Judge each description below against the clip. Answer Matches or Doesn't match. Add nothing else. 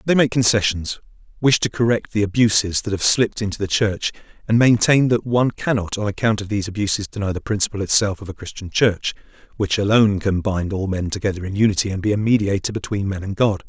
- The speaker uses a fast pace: Matches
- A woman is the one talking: Doesn't match